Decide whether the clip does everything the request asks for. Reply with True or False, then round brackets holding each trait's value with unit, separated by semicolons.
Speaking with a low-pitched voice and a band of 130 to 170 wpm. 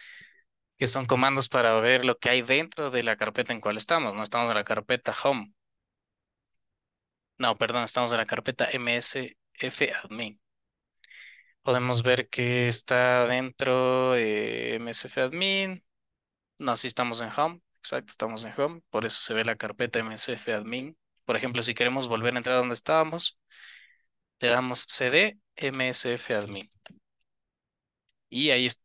True (125 Hz; 150 wpm)